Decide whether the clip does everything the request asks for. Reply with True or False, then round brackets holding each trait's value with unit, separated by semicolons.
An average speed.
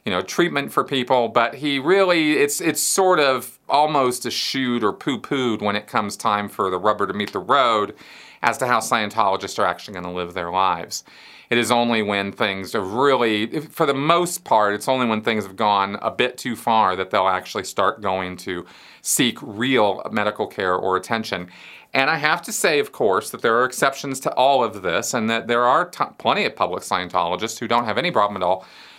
False (215 wpm)